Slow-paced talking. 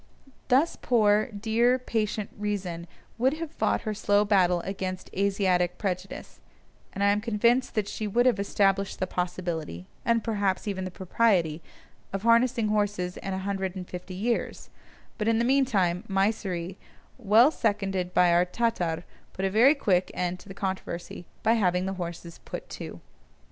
No: average, 160 wpm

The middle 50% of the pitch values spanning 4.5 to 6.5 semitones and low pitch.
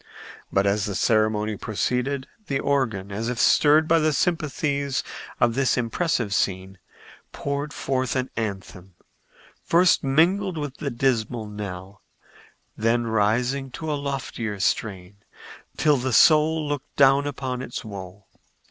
Yes: average, 5.2 semitones; low, 125 Hz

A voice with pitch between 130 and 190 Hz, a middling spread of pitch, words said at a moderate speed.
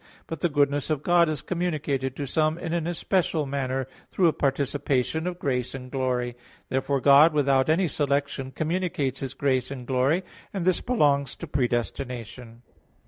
Yes: medium, 140 Hz; average, 3.4 semitones; average, 160 wpm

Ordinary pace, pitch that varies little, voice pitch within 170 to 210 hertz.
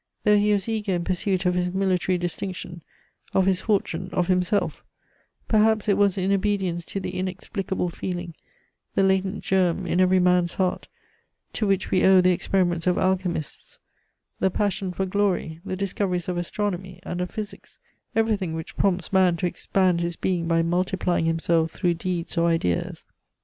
Yes: average, 165 wpm; narrow, 1.8 semitones; medium, 185 Hz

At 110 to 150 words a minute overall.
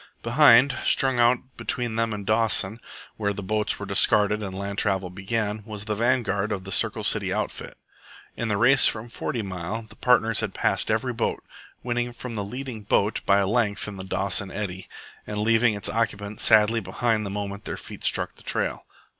No: average, 190 wpm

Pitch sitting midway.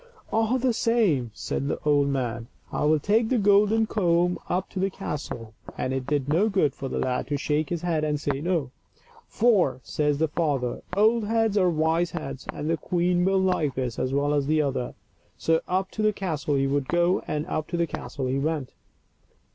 Yes: medium, 160 Hz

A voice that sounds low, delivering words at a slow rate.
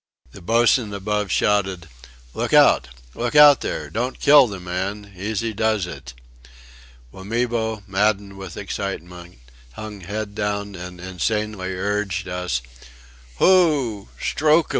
Yes: low, 100 Hz; slow, 120 wpm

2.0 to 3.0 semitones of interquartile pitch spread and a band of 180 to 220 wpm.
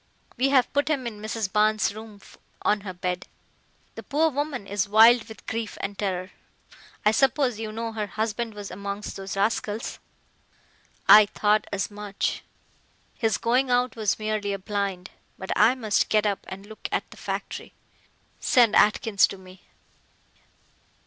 No: narrow, 2.4 semitones; average, 155 wpm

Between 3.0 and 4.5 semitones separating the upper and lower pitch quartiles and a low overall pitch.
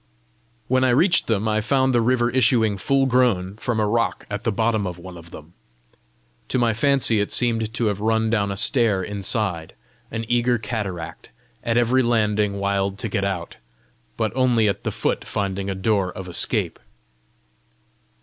Yes: average, 3.4 semitones; low, 110 Hz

